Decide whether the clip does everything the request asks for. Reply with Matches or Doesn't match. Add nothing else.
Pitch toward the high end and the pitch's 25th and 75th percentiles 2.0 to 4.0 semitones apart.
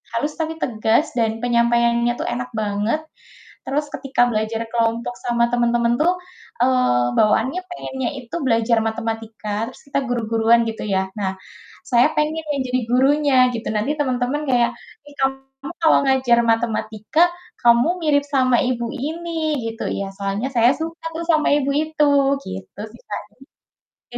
Matches